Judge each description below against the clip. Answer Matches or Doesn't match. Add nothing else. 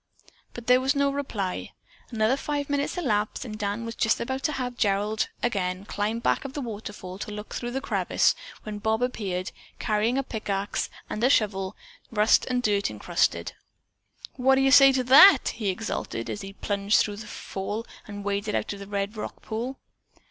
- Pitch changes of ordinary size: Matches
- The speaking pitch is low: Doesn't match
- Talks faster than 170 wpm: Matches